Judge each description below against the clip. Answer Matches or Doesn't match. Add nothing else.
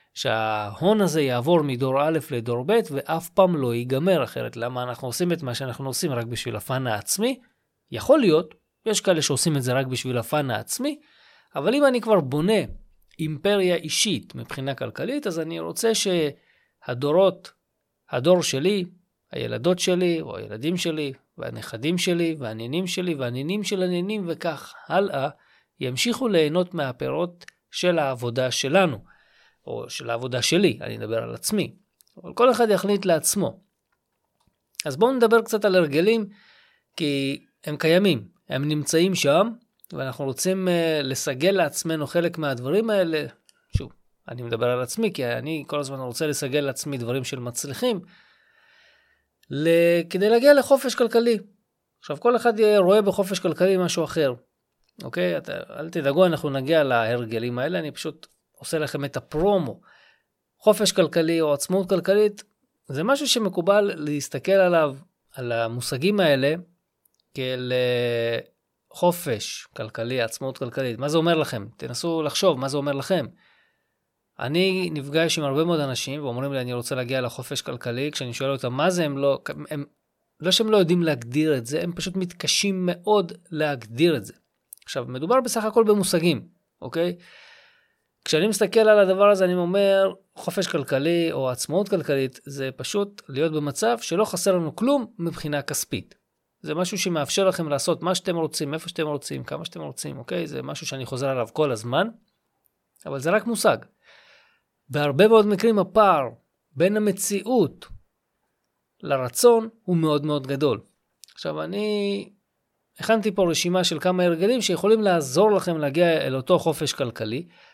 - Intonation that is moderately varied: Doesn't match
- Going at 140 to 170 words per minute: Matches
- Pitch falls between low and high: Matches